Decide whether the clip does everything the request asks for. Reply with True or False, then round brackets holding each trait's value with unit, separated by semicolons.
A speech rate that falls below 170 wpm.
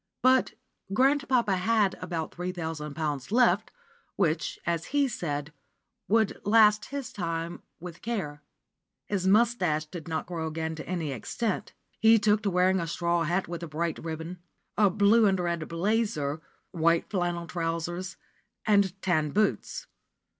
True (145 wpm)